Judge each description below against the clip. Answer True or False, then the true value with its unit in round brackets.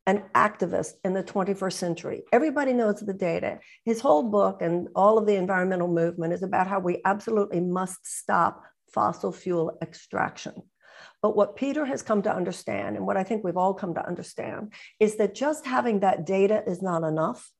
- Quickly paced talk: False (185 wpm)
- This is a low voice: False (195 Hz)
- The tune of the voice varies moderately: True (3.1 semitones)